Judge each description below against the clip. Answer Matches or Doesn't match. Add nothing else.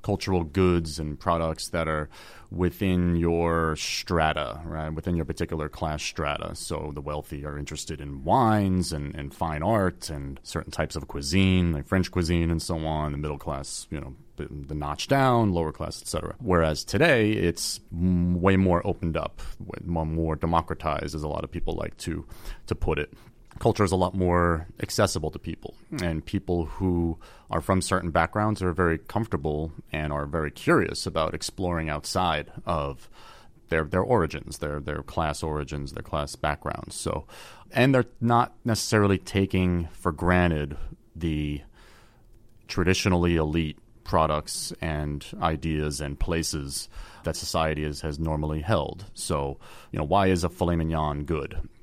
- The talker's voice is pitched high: Doesn't match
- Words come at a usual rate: Matches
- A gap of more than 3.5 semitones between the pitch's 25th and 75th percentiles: Doesn't match